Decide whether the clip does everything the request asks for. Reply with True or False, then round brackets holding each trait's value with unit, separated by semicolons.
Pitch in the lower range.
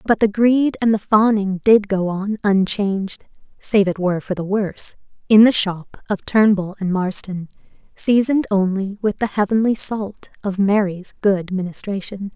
False (200 Hz)